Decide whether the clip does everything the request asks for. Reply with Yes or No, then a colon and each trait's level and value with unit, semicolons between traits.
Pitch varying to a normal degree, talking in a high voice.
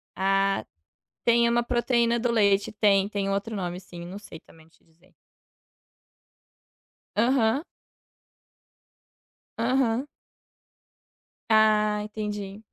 Yes: average, 3.2 semitones; high, 210 Hz